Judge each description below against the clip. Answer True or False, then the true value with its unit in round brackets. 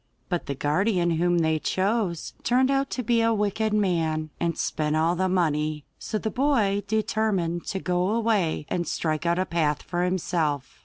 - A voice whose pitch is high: False (180 Hz)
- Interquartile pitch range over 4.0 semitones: True (4.9 semitones)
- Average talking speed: True (175 wpm)